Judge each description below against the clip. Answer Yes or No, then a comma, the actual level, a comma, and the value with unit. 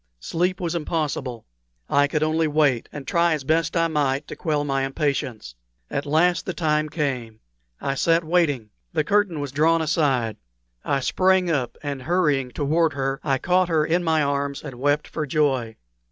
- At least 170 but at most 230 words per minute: Yes, average, 175 wpm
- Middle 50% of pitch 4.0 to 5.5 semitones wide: No, average, 3.3 semitones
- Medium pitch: Yes, medium, 150 Hz